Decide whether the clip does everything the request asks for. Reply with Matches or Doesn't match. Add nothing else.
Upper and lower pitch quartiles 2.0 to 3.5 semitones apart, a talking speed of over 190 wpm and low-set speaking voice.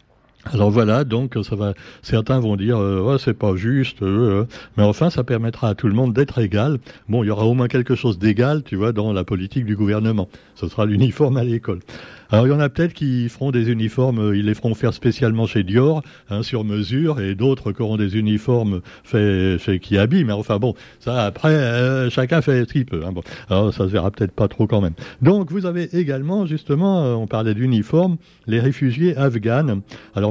Doesn't match